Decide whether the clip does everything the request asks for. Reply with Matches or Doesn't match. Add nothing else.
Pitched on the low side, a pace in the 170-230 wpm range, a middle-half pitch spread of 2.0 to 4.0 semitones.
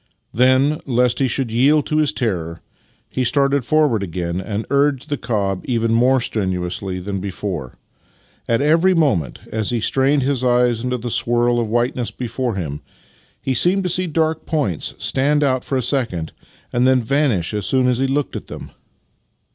Doesn't match